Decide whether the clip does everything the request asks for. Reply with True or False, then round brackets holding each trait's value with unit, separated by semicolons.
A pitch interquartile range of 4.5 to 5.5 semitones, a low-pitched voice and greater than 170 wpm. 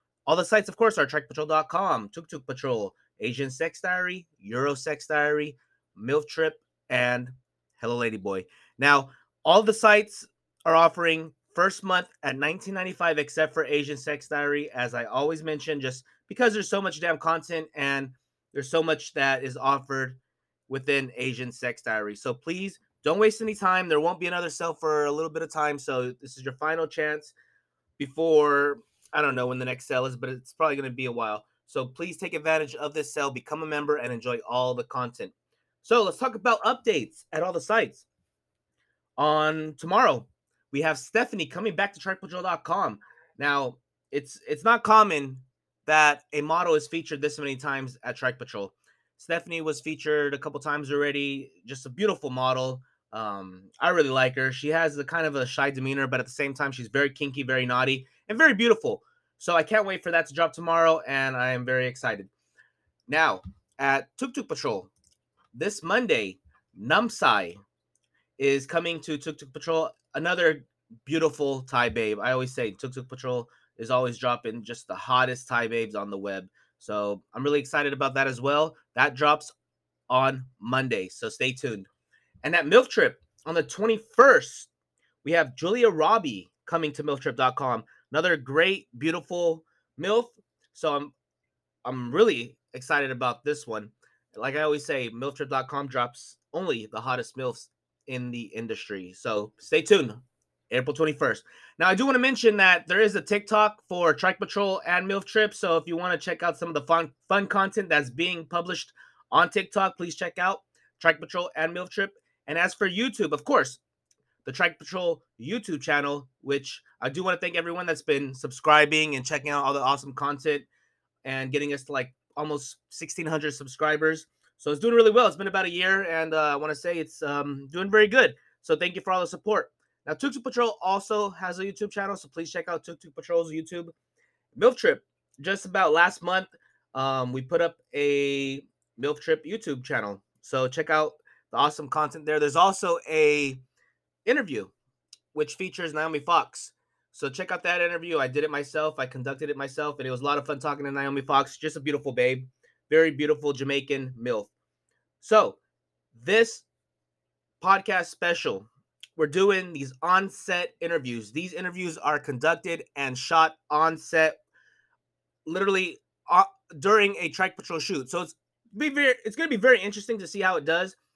False (4.9 semitones; 150 Hz; 180 wpm)